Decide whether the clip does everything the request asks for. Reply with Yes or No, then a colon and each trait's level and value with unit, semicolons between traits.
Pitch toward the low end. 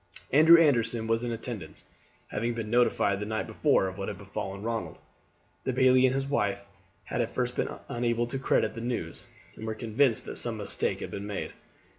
Yes: low, 115 Hz